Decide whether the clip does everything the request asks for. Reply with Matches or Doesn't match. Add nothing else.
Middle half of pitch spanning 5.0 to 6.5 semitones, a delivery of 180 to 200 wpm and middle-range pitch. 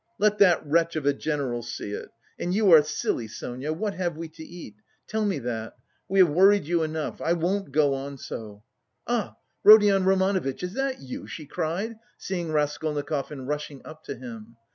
Matches